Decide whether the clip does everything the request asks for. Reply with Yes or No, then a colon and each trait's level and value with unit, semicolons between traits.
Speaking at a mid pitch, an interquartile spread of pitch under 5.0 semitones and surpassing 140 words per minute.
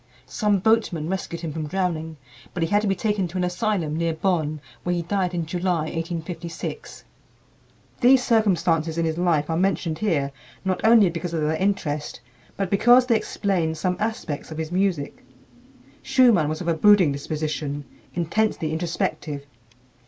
Yes: medium, 170 Hz; average, 3.7 semitones; average, 160 wpm